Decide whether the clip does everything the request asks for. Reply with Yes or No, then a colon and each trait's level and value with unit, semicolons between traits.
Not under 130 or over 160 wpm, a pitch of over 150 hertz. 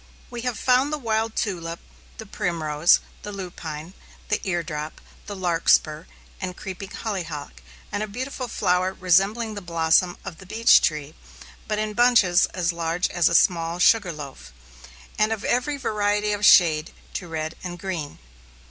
Yes: average, 155 wpm; medium, 185 Hz